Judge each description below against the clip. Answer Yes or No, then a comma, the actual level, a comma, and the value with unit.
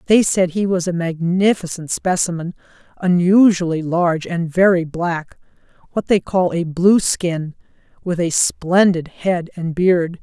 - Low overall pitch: No, medium, 175 Hz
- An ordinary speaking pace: No, slow, 125 wpm